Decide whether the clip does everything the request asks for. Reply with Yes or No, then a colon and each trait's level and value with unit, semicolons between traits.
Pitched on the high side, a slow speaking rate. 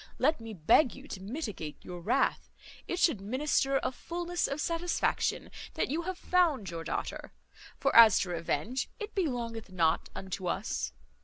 No: high, 245 Hz; average, 160 wpm